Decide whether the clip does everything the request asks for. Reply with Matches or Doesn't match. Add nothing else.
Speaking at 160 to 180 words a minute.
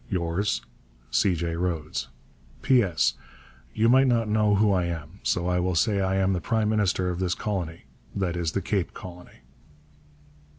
Matches